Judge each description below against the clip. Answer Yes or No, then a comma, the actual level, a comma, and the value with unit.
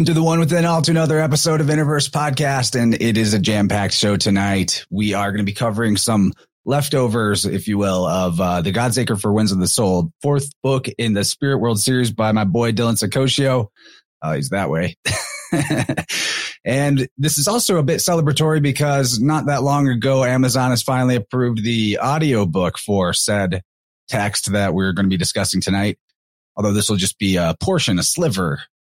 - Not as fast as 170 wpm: No, average, 190 wpm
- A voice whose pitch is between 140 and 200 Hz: No, low, 120 Hz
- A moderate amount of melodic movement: No, wide, 5.7 semitones